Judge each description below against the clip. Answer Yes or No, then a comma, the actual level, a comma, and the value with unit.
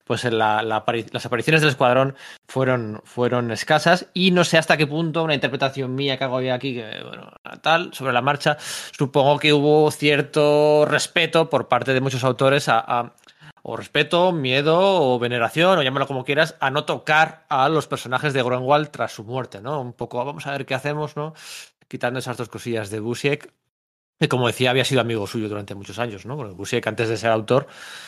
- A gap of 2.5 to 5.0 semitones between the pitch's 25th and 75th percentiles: Yes, average, 3.8 semitones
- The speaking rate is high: Yes, fast, 200 wpm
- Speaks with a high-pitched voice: No, low, 135 Hz